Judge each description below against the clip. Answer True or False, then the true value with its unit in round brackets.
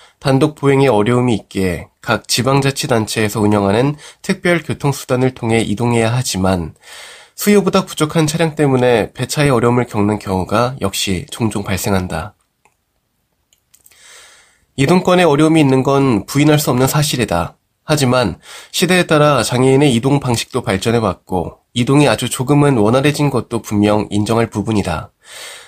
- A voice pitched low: True (125 Hz)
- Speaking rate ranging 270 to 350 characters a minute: True (325 characters per minute)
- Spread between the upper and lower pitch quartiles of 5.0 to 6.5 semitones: True (5.6 semitones)